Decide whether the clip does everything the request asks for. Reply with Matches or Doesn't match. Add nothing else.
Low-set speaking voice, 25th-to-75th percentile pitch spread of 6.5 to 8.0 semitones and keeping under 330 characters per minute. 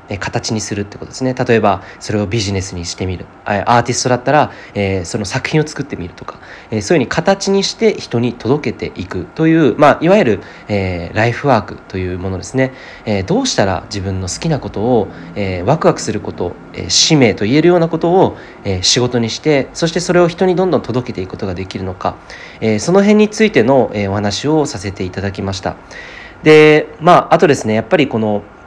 Doesn't match